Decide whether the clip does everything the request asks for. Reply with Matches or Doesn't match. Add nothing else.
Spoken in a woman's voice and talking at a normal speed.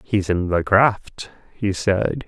Doesn't match